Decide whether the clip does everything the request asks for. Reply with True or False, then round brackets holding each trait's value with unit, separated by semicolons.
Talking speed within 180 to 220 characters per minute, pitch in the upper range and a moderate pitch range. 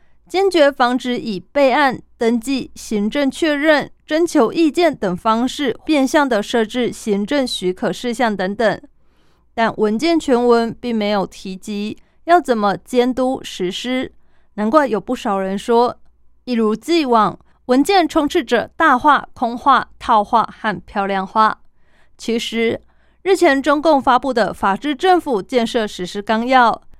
True (210 characters per minute; 240 Hz; 5.0 semitones)